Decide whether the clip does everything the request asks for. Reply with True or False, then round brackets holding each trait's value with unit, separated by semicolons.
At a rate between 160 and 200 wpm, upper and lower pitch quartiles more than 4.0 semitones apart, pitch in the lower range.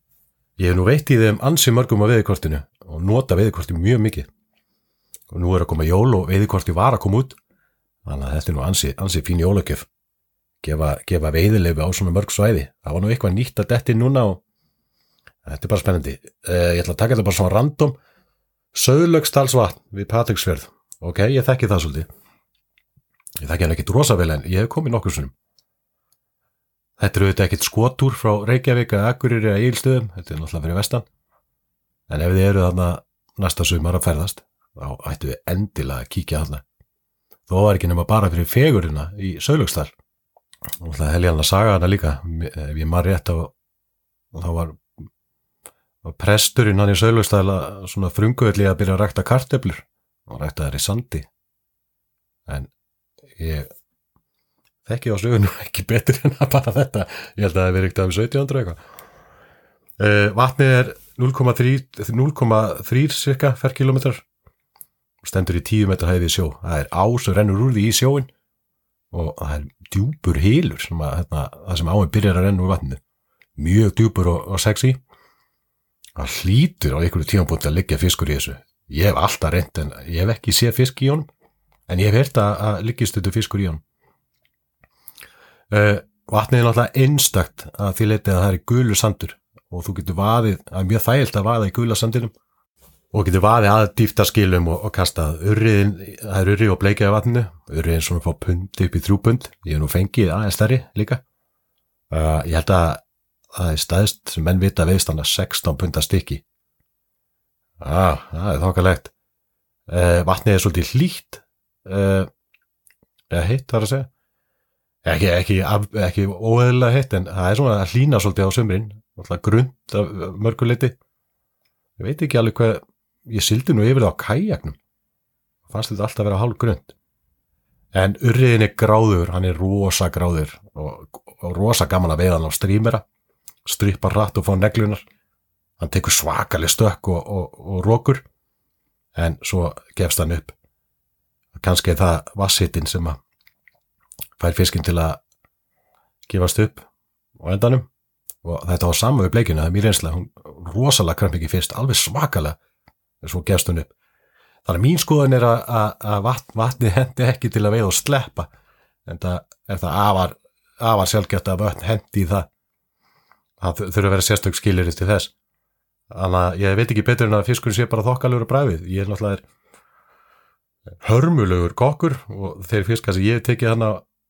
True (170 wpm; 4.6 semitones; 100 Hz)